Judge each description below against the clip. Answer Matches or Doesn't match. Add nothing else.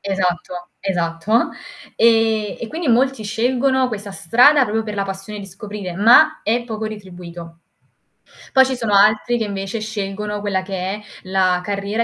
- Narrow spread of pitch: Doesn't match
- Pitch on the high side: Matches